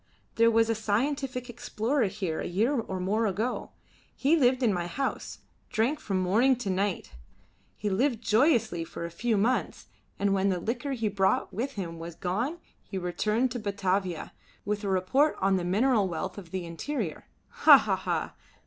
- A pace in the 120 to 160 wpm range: No, average, 175 wpm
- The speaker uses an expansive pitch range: No, average, 4.7 semitones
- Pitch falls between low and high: No, high, 210 Hz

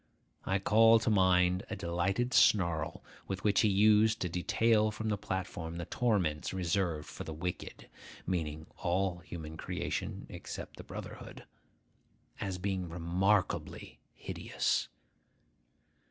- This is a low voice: Yes, very low, 95 Hz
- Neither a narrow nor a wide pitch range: Yes, average, 3.3 semitones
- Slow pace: Yes, slow, 125 wpm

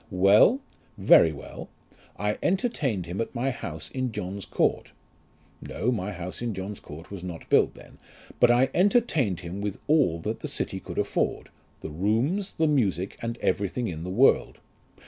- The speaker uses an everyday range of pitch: No, wide, 6.1 semitones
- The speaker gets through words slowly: No, average, 165 wpm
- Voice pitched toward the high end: No, low, 105 Hz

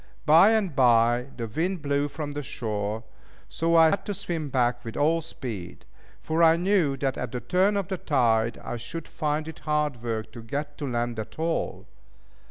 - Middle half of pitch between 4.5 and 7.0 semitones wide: Yes, wide, 5.6 semitones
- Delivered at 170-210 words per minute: Yes, average, 190 wpm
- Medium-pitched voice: Yes, medium, 145 Hz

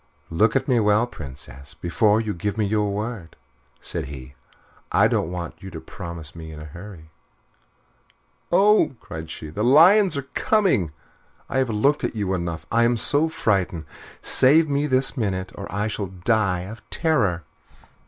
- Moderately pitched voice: No, low, 105 Hz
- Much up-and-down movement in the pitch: Yes, wide, 7.1 semitones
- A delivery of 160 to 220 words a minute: Yes, average, 165 wpm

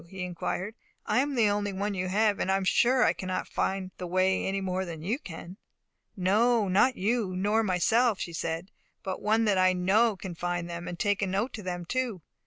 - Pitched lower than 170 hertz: No, high, 190 Hz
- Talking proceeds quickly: Yes, fast, 220 wpm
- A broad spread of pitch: No, average, 2.9 semitones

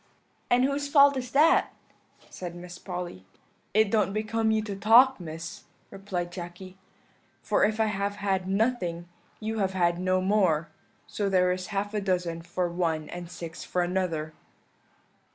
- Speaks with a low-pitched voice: No, high, 190 Hz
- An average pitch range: Yes, average, 3.6 semitones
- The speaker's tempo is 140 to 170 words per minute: Yes, average, 155 wpm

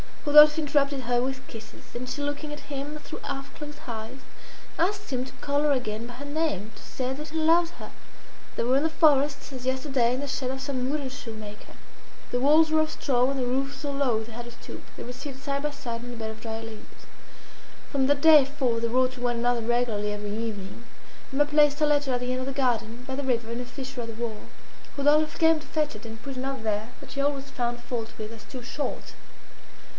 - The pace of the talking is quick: Yes, fast, 235 wpm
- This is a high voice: Yes, very high, 260 Hz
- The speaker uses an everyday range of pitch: Yes, average, 3.4 semitones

